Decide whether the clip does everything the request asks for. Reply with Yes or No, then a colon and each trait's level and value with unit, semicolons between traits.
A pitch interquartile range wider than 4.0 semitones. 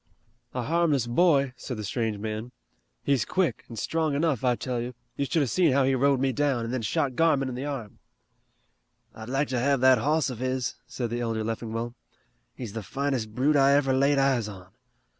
No: average, 3.2 semitones